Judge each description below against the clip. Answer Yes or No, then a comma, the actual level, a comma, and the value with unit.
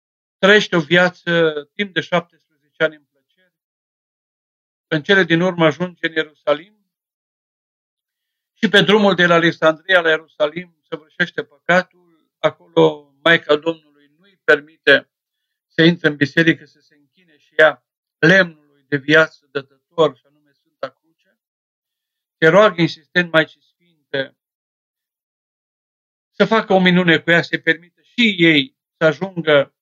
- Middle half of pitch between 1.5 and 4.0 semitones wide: Yes, average, 3.0 semitones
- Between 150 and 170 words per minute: No, average, 135 wpm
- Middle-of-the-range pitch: Yes, medium, 160 Hz